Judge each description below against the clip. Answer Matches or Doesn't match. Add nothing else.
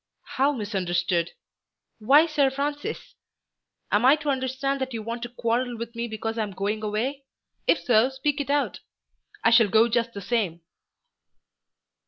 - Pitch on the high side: Matches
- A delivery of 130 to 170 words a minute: Matches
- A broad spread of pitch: Doesn't match